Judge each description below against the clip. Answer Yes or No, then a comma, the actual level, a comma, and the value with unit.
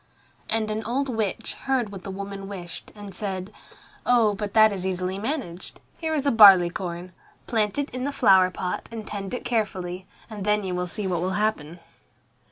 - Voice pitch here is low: No, high, 200 Hz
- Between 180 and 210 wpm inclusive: Yes, average, 190 wpm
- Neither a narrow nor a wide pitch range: Yes, average, 3.2 semitones